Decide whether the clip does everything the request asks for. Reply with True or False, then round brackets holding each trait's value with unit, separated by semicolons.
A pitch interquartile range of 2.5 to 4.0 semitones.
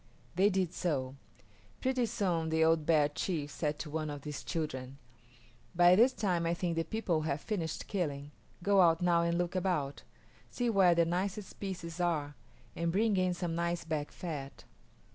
True (3.1 semitones)